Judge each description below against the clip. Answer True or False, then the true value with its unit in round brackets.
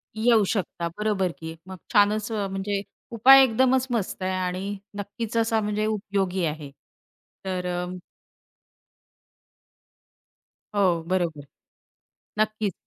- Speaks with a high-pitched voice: True (205 Hz)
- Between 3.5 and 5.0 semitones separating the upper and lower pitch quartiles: False (2.7 semitones)